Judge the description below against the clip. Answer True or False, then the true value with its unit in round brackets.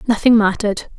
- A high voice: True (215 Hz)